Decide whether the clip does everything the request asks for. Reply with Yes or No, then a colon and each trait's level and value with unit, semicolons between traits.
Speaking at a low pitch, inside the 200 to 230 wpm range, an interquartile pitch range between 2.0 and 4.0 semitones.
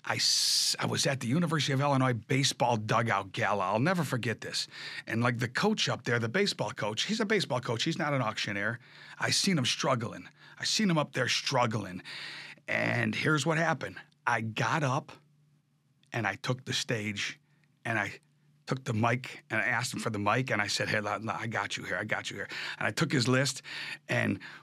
No: low, 130 Hz; fast, 205 wpm; average, 4.5 semitones